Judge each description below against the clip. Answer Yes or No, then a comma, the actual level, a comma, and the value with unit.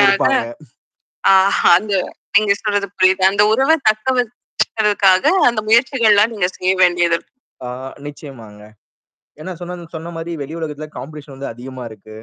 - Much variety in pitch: Yes, wide, 5.8 semitones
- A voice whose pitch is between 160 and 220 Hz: Yes, medium, 185 Hz